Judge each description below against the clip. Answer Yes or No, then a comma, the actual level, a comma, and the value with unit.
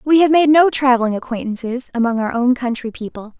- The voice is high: Yes, very high, 250 Hz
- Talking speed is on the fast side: No, average, 195 wpm